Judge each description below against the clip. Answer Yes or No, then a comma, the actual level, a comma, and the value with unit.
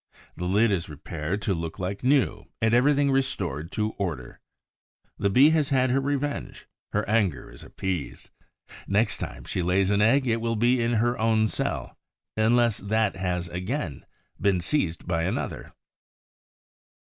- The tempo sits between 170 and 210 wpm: No, average, 155 wpm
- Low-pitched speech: Yes, low, 105 Hz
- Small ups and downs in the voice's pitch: No, average, 5.1 semitones